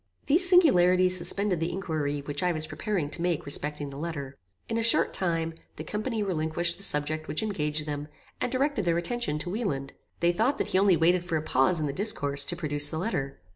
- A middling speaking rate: No, fast, 215 wpm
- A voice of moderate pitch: Yes, medium, 170 Hz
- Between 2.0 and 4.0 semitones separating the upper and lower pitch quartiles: No, average, 4.9 semitones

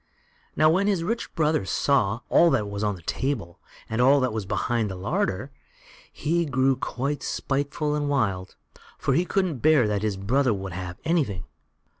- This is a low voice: Yes, low, 130 Hz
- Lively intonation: Yes, wide, 6.7 semitones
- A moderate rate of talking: Yes, average, 180 wpm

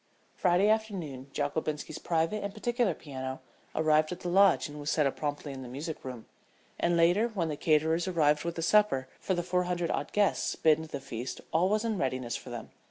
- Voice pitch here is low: No, medium, 160 Hz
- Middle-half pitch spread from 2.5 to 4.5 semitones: Yes, average, 4.2 semitones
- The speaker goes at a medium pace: No, fast, 210 wpm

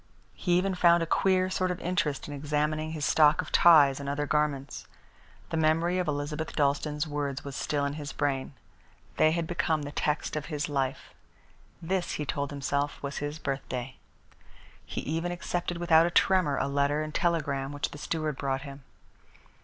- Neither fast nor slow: Yes, average, 175 wpm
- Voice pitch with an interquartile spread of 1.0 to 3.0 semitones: Yes, narrow, 2.6 semitones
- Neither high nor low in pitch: Yes, medium, 150 Hz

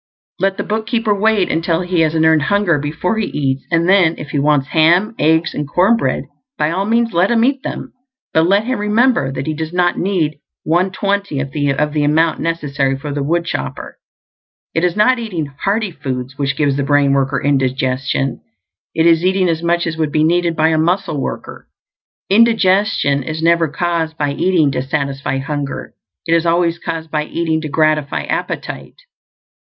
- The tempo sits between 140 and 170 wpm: No, average, 185 wpm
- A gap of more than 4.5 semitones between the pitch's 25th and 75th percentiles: No, average, 4.2 semitones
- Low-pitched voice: No, medium, 160 Hz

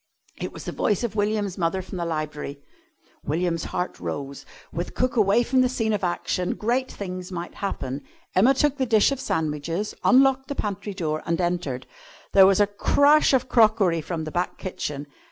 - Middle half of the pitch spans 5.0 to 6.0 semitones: Yes, wide, 5.6 semitones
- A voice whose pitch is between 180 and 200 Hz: Yes, high, 190 Hz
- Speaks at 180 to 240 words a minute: Yes, average, 185 wpm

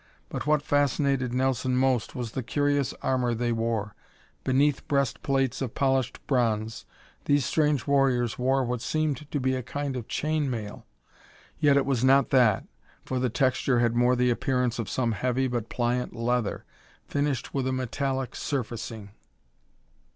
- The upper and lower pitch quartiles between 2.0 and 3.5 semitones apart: Yes, narrow, 2.4 semitones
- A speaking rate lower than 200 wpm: Yes, average, 160 wpm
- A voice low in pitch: Yes, low, 130 Hz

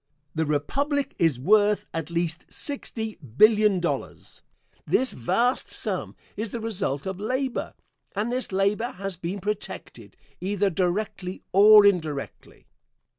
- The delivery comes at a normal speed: No, slow, 125 wpm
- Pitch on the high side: Yes, high, 200 Hz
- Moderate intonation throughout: Yes, average, 3.8 semitones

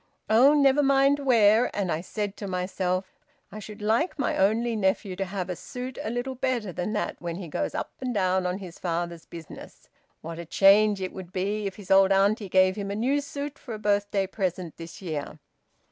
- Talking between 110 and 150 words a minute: No, fast, 205 wpm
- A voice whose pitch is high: Yes, high, 200 Hz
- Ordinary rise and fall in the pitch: Yes, average, 3.8 semitones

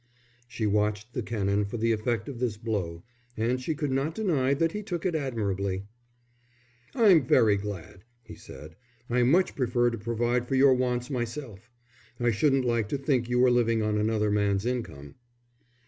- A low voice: Yes, low, 120 Hz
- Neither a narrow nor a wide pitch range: Yes, average, 3.8 semitones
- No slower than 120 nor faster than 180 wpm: Yes, average, 175 wpm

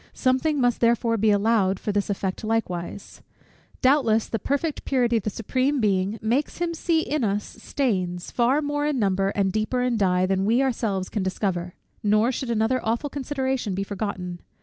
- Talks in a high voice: Yes, high, 225 Hz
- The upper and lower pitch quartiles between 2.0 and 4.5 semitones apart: No, average, 4.9 semitones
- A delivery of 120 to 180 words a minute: Yes, average, 175 wpm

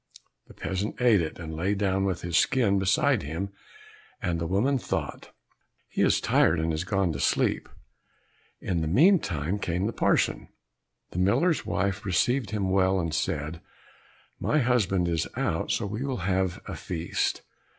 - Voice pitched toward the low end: Yes, very low, 95 Hz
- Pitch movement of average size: Yes, average, 3.8 semitones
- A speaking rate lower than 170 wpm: Yes, average, 160 wpm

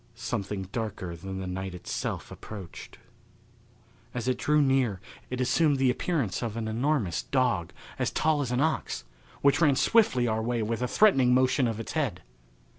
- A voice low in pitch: Yes, low, 125 Hz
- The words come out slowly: No, average, 170 wpm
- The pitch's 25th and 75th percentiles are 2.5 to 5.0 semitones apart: Yes, average, 4.1 semitones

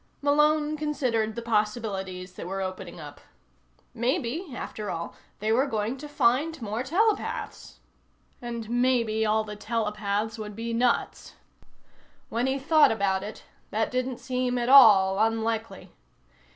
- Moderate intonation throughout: Yes, average, 3.4 semitones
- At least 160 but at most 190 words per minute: No, slow, 135 wpm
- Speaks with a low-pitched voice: No, high, 230 Hz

